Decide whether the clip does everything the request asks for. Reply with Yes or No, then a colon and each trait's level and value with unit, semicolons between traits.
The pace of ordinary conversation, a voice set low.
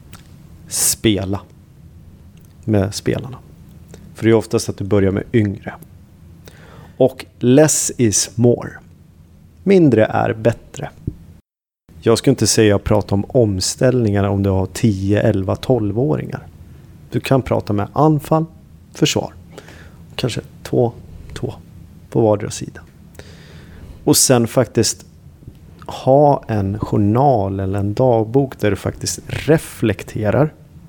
No: slow, 115 wpm; low, 105 Hz